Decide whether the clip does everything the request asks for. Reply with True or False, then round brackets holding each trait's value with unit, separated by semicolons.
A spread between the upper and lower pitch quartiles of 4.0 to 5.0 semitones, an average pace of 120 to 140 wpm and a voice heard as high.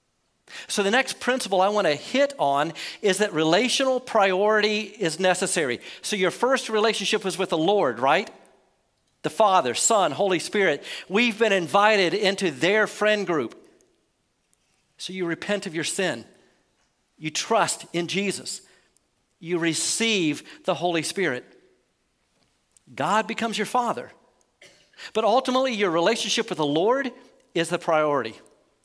True (4.3 semitones; 135 wpm; 200 Hz)